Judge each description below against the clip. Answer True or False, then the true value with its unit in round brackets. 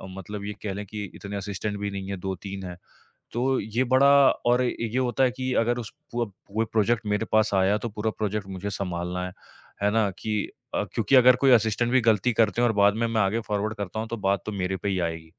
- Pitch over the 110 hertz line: False (105 Hz)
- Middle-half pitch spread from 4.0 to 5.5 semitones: False (2.9 semitones)